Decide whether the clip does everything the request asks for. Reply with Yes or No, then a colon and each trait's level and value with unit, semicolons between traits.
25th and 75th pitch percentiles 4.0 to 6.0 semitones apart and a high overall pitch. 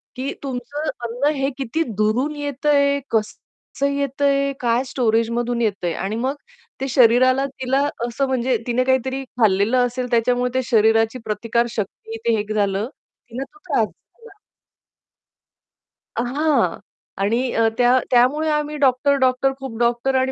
No: average, 3.0 semitones; very high, 255 Hz